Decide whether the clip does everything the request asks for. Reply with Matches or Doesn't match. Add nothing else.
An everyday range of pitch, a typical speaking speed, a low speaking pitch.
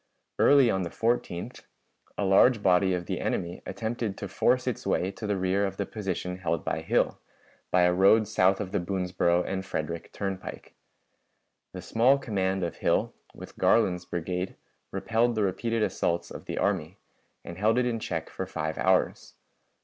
Matches